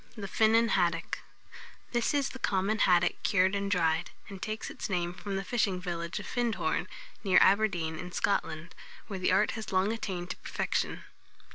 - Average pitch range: Yes, average, 3.4 semitones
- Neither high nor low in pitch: No, high, 195 Hz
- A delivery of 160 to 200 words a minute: Yes, average, 170 wpm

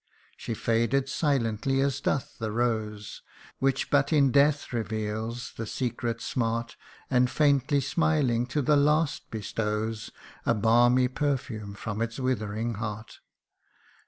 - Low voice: Yes, low, 120 Hz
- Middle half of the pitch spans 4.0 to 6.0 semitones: No, average, 3.6 semitones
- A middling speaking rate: No, slow, 125 wpm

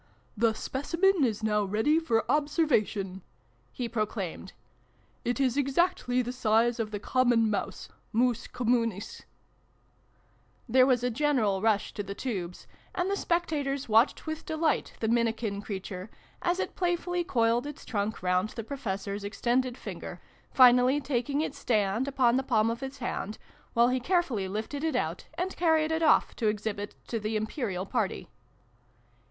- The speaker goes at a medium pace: Yes, average, 160 wpm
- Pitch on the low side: No, high, 240 Hz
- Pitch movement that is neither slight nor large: Yes, average, 4.8 semitones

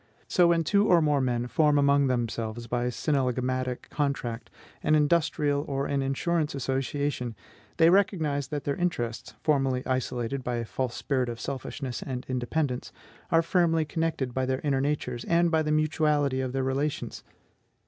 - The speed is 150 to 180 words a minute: Yes, average, 160 wpm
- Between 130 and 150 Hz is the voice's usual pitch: Yes, medium, 140 Hz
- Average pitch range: Yes, average, 3.3 semitones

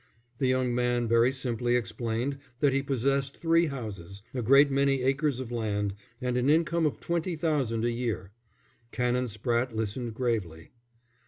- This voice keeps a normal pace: Yes, average, 155 wpm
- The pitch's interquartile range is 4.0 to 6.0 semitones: No, average, 3.1 semitones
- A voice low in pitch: Yes, low, 125 Hz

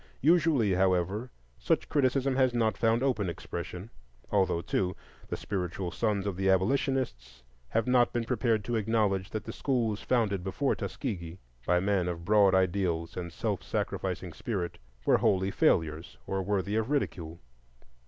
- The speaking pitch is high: No, low, 100 Hz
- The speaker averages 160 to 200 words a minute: No, average, 150 wpm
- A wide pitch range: No, average, 4.5 semitones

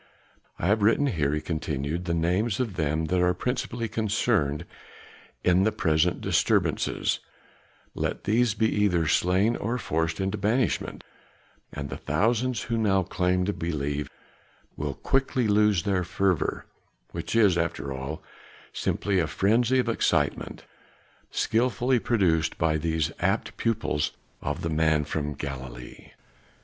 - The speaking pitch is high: No, very low, 90 Hz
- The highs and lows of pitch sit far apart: Yes, wide, 6.0 semitones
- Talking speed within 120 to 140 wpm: Yes, slow, 135 wpm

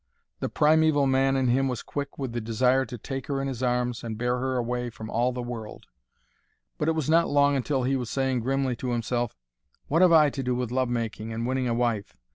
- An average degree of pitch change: No, narrow, 2.1 semitones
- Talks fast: Yes, fast, 235 wpm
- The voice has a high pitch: No, low, 125 Hz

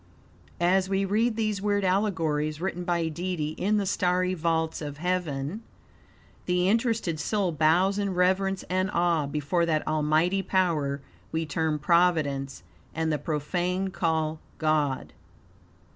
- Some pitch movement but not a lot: Yes, average, 3.5 semitones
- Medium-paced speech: No, slow, 130 wpm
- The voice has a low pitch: No, medium, 175 Hz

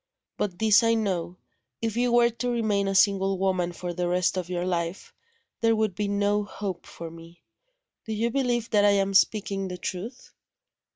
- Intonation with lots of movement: No, average, 3.4 semitones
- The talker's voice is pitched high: Yes, high, 200 Hz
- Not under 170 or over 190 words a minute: Yes, average, 185 wpm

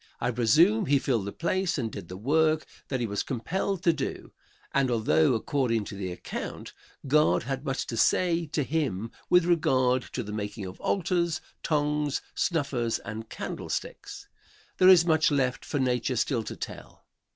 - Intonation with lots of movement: Yes, wide, 5.7 semitones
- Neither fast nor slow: Yes, average, 170 wpm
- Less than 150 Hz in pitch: Yes, low, 135 Hz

